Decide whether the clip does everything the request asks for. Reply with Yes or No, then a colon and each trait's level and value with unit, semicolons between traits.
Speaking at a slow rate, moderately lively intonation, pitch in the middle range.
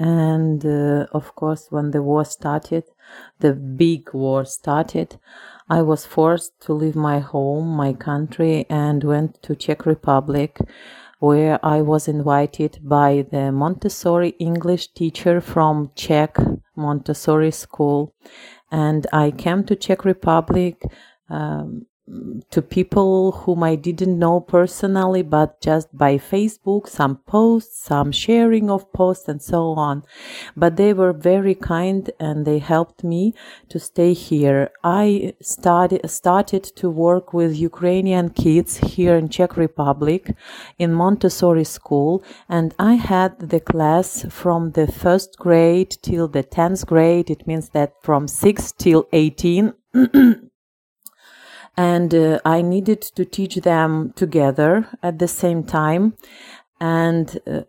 Yes: slow, 130 wpm; average, 3.3 semitones; medium, 165 Hz